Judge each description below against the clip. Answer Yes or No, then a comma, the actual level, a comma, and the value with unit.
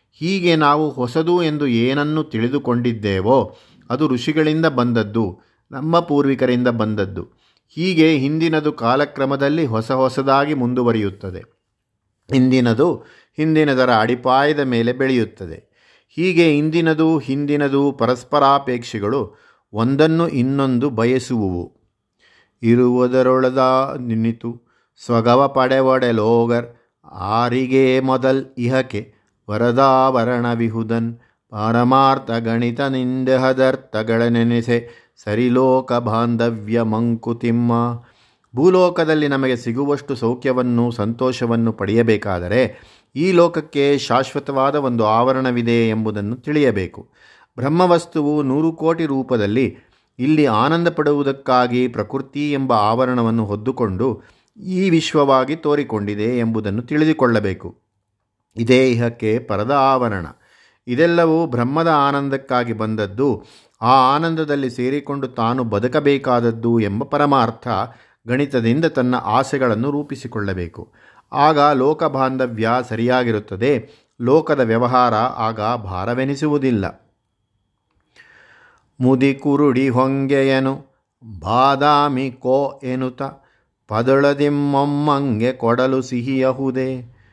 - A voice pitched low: Yes, low, 125 Hz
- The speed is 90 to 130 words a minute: No, average, 75 wpm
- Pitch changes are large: No, average, 3.3 semitones